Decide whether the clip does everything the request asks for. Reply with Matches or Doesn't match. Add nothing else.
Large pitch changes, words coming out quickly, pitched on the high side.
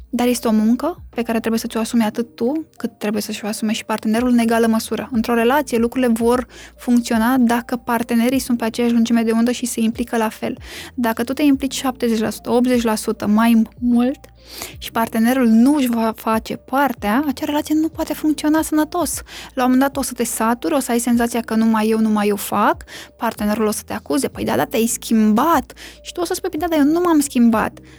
Doesn't match